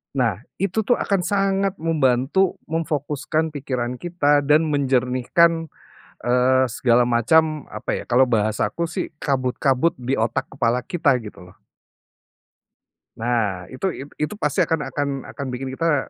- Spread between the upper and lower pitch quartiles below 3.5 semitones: No, average, 4.7 semitones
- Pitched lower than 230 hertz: Yes, medium, 140 Hz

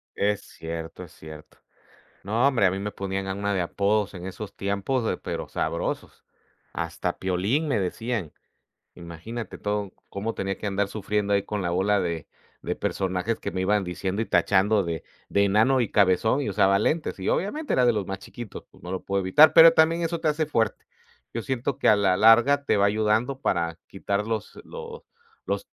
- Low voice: Yes, low, 100 Hz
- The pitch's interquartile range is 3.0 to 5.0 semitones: Yes, average, 3.7 semitones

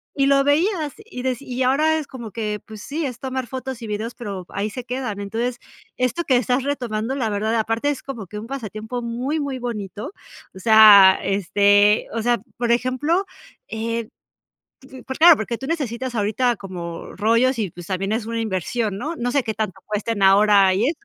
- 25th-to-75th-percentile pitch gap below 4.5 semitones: Yes, average, 3.8 semitones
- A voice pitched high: Yes, high, 235 Hz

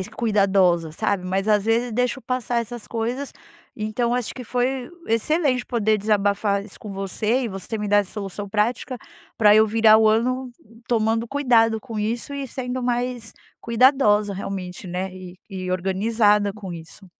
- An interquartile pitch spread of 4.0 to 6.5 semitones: No, average, 3.4 semitones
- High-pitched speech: Yes, high, 220 Hz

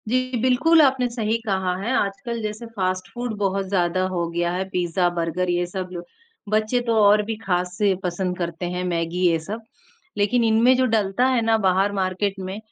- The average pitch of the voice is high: Yes, high, 195 Hz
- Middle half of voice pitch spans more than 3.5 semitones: Yes, average, 3.9 semitones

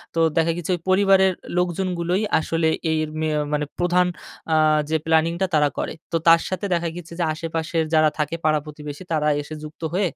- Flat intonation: Yes, narrow, 2.2 semitones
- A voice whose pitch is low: No, medium, 165 Hz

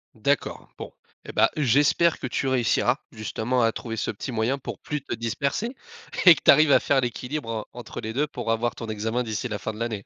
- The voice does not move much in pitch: No, average, 3.8 semitones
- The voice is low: Yes, low, 120 Hz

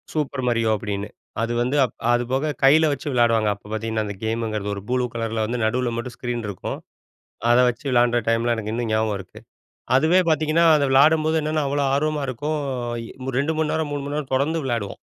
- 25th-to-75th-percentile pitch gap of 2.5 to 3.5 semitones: No, average, 4.2 semitones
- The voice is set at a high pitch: No, low, 125 Hz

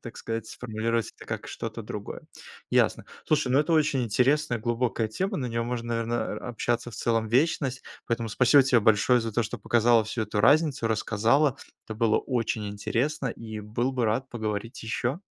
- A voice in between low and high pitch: No, low, 120 Hz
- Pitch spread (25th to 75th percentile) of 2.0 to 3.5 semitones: Yes, average, 2.7 semitones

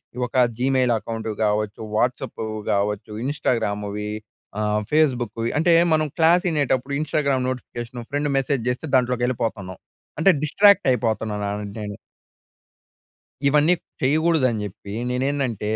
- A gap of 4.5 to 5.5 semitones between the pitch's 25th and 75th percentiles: Yes, average, 4.9 semitones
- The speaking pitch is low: Yes, low, 125 Hz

